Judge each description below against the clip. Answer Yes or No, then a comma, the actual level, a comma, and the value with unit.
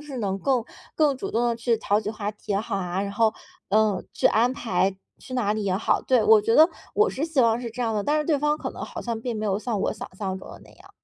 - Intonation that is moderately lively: Yes, average, 3.5 semitones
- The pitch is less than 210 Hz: No, high, 225 Hz